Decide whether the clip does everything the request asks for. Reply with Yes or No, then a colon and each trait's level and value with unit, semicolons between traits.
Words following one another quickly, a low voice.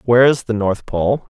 Yes: fast, 220 wpm; low, 115 Hz